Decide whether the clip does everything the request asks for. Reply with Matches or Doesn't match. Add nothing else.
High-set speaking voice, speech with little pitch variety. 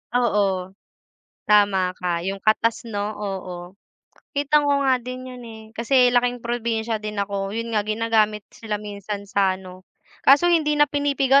Doesn't match